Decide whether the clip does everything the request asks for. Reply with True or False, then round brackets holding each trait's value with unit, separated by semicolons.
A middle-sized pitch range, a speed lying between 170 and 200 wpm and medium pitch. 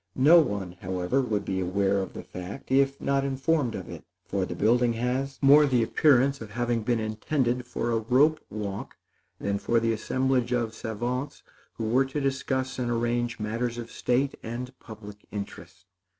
False (3.7 semitones; 175 wpm; 120 Hz)